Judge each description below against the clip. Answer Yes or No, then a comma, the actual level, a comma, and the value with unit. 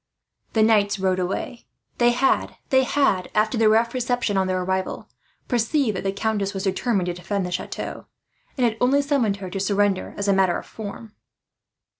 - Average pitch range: Yes, average, 3.7 semitones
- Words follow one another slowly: No, average, 175 wpm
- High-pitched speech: Yes, high, 205 Hz